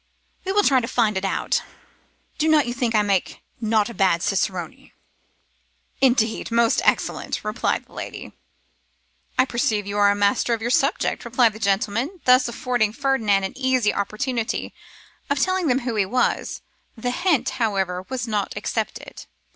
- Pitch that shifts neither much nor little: Yes, average, 3.9 semitones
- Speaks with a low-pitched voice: No, high, 230 Hz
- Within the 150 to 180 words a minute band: Yes, average, 165 wpm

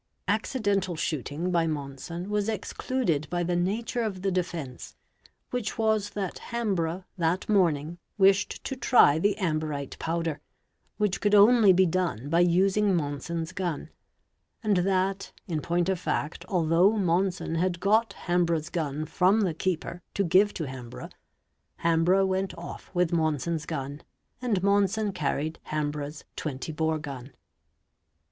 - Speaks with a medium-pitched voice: Yes, medium, 175 Hz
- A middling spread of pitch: Yes, average, 3.8 semitones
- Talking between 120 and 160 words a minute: Yes, average, 140 wpm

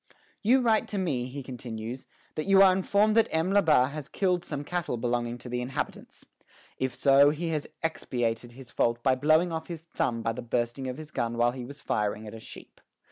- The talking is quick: Yes, fast, 215 wpm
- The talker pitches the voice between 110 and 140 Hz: Yes, low, 135 Hz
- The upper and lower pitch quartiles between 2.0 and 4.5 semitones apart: No, average, 5.3 semitones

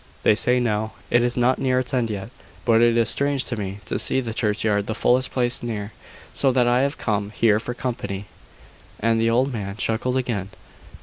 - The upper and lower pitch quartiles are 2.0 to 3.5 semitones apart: Yes, average, 2.9 semitones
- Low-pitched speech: Yes, low, 115 Hz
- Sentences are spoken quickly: Yes, fast, 210 wpm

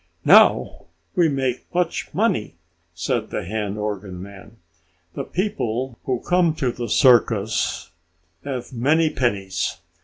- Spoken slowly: Yes, slow, 120 wpm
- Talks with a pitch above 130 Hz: No, low, 120 Hz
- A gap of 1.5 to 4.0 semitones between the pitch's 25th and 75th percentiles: No, average, 5.3 semitones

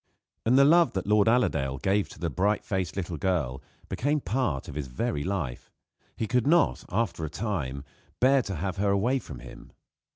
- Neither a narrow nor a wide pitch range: No, wide, 7.3 semitones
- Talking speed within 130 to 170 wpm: No, average, 190 wpm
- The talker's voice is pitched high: No, low, 100 Hz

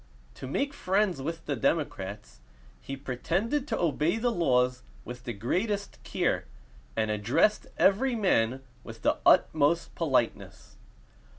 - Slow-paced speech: Yes, slow, 125 wpm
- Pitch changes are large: Yes, wide, 8.1 semitones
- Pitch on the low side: No, medium, 150 Hz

